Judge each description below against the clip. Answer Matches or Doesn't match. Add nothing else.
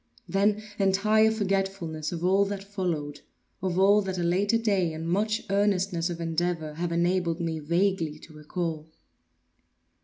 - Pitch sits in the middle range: Matches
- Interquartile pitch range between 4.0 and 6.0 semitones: Doesn't match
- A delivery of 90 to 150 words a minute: Matches